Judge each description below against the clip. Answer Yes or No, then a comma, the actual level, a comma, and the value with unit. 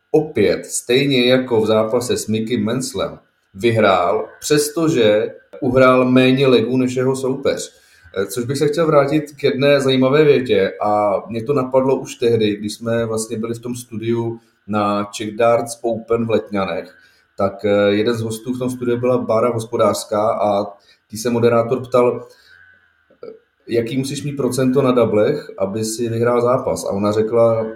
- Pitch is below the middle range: Yes, low, 120 Hz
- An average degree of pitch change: Yes, average, 3.1 semitones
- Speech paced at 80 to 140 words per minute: No, average, 155 wpm